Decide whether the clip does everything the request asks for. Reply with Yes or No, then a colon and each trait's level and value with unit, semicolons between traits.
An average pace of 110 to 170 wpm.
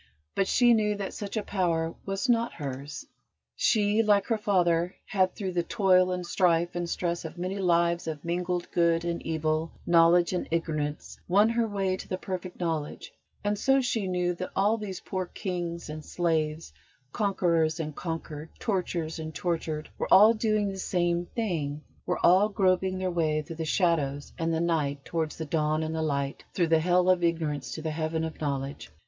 No: average, 185 wpm